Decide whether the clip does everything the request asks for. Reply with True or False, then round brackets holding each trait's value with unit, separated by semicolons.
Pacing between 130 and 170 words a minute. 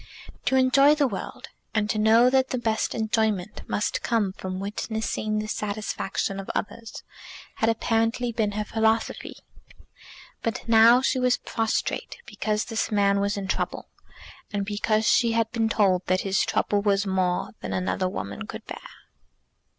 True (155 wpm)